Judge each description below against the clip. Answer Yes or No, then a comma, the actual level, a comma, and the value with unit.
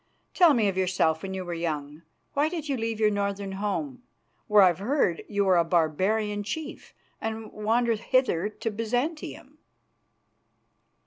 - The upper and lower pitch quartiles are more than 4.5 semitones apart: No, average, 3.8 semitones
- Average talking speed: Yes, average, 150 wpm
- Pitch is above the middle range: Yes, high, 210 Hz